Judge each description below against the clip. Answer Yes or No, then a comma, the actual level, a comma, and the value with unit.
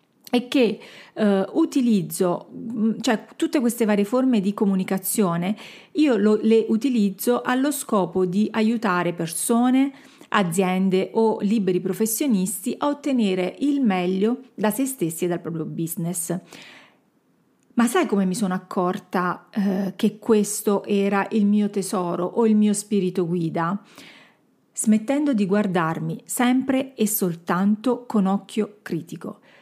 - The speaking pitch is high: Yes, high, 210 Hz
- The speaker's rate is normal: Yes, average, 125 wpm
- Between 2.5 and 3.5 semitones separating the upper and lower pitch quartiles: No, average, 4.0 semitones